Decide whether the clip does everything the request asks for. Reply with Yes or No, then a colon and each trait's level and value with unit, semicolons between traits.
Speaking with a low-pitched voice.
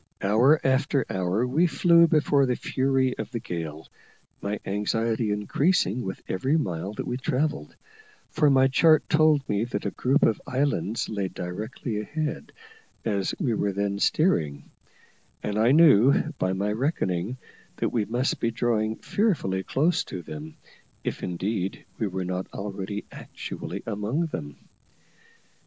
Yes: low, 115 Hz